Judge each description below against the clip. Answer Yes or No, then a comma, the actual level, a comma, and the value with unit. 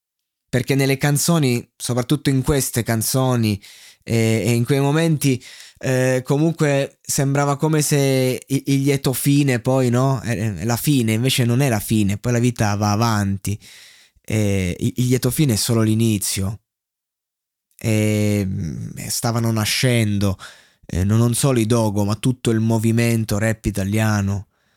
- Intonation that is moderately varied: Yes, average, 3.9 semitones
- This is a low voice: Yes, low, 120 Hz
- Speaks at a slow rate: No, average, 140 wpm